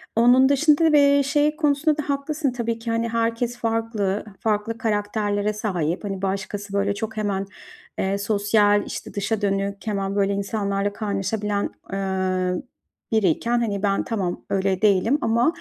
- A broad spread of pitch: No, average, 2.8 semitones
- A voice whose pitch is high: Yes, high, 210 Hz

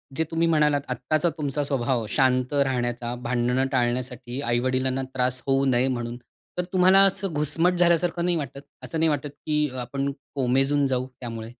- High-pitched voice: No, low, 135 Hz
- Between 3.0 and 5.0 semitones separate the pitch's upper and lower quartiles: Yes, average, 3.3 semitones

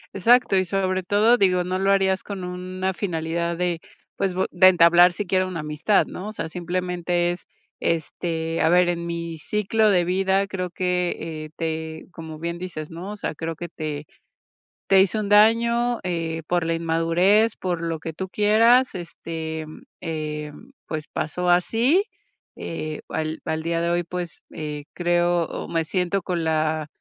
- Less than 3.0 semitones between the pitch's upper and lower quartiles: Yes, narrow, 2.5 semitones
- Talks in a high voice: No, medium, 175 Hz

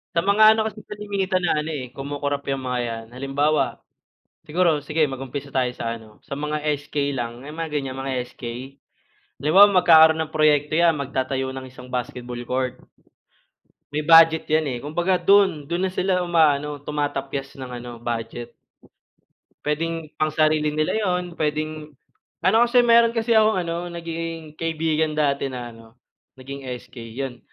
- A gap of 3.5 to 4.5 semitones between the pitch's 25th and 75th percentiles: Yes, average, 3.8 semitones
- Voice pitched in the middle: Yes, medium, 150 Hz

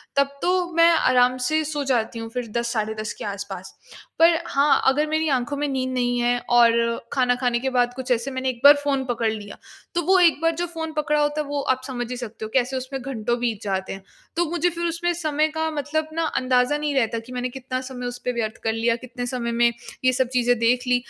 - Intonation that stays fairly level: No, average, 3.6 semitones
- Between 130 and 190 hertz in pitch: No, very high, 255 Hz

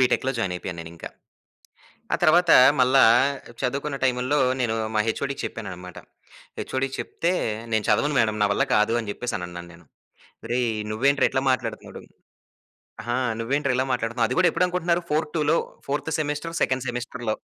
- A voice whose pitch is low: Yes, low, 125 Hz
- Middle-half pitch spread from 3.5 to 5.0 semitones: Yes, average, 4.7 semitones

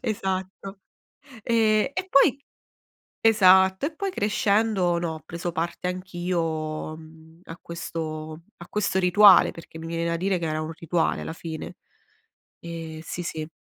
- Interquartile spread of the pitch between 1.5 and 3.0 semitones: No, average, 3.4 semitones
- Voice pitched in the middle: Yes, medium, 175 Hz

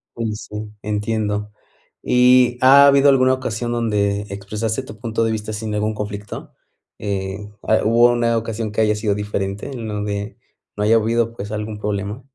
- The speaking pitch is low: Yes, low, 110 Hz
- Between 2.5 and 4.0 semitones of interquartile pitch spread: No, narrow, 2.0 semitones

